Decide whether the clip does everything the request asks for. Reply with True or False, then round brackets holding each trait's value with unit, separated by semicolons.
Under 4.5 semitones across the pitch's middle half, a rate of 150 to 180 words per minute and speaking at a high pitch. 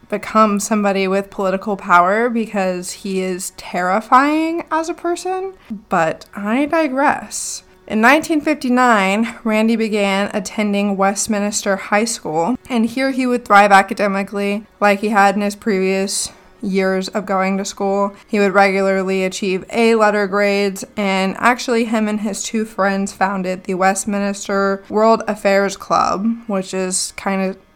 False (2.6 semitones; 140 wpm; 205 Hz)